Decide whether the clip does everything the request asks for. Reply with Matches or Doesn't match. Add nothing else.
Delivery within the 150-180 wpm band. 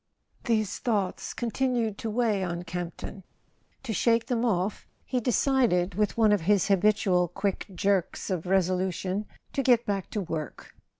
Matches